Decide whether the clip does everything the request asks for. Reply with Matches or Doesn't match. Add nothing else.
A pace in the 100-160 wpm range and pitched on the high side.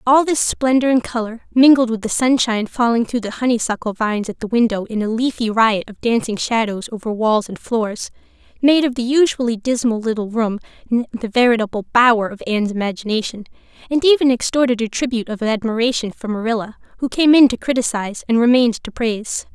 Doesn't match